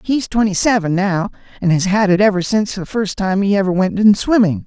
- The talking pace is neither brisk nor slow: No, fast, 230 wpm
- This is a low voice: No, high, 195 Hz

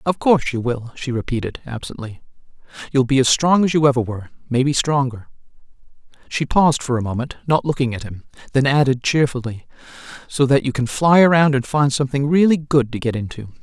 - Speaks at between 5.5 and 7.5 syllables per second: Yes, 6.0 syllables/s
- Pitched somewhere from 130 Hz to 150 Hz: Yes, low, 135 Hz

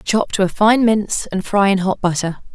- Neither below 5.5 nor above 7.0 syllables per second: No, 5.0 syllables/s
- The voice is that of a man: No, female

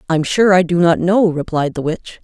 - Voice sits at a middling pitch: Yes, medium, 175 Hz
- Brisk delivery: Yes, fast, 240 wpm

